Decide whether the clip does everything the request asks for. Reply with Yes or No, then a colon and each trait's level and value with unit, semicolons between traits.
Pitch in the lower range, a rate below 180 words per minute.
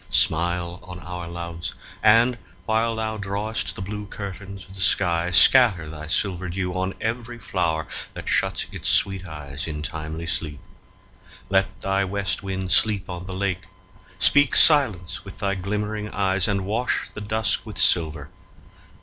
Yes: very low, 95 Hz; average, 155 wpm